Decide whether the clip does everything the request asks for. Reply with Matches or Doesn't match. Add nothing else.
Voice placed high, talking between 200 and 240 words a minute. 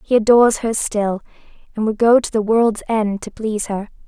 Matches